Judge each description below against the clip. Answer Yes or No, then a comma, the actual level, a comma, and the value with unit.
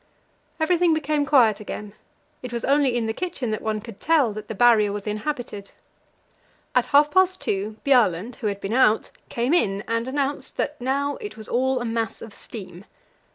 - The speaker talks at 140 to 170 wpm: No, average, 185 wpm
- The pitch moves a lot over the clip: No, average, 4.8 semitones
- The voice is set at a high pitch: Yes, high, 235 Hz